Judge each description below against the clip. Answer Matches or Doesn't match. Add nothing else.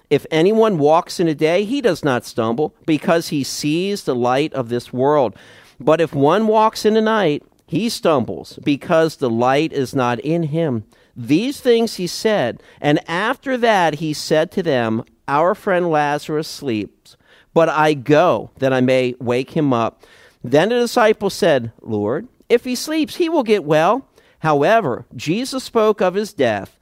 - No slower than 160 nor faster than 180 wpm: Matches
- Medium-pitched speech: Matches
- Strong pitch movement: Matches